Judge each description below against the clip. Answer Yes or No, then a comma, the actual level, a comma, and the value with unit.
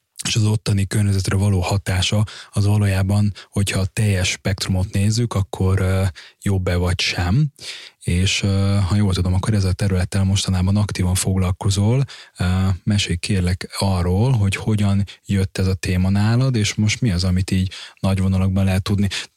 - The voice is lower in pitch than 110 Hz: Yes, low, 100 Hz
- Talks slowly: No, average, 150 wpm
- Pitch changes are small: Yes, narrow, 1.7 semitones